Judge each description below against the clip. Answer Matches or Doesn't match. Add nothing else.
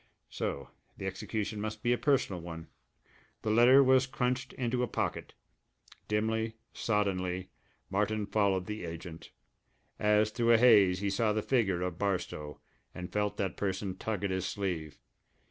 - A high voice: Doesn't match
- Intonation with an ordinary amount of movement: Matches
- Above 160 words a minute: Doesn't match